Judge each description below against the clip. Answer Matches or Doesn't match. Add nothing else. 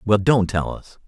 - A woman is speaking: Doesn't match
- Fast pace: Matches